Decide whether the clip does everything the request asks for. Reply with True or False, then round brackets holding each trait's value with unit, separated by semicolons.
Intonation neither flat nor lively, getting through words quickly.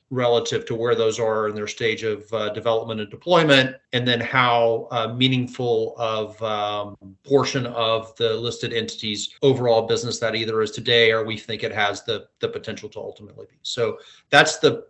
False (3.2 semitones; 180 wpm)